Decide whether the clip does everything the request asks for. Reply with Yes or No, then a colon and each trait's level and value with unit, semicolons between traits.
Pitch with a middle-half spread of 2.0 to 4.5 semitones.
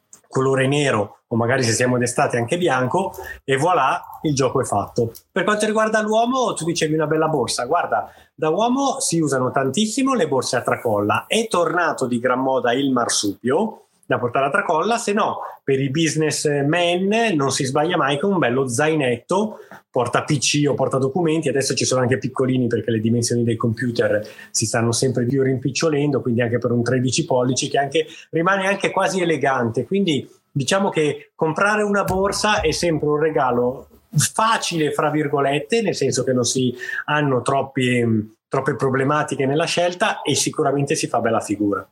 No: average, 5.3 semitones